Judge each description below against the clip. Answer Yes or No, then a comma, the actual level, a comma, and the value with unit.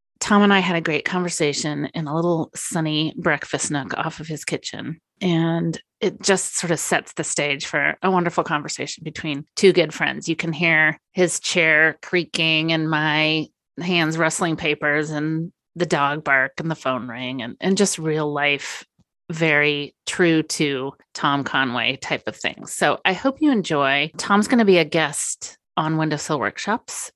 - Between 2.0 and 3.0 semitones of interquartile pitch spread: Yes, average, 2.7 semitones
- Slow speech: No, average, 175 wpm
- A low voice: No, medium, 160 Hz